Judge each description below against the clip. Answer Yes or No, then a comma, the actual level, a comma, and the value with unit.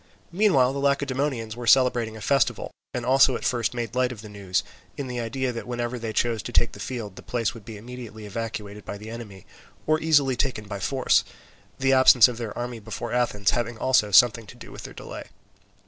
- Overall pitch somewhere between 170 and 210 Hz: No, low, 120 Hz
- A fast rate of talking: Yes, fast, 210 wpm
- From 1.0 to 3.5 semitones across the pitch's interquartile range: Yes, average, 2.9 semitones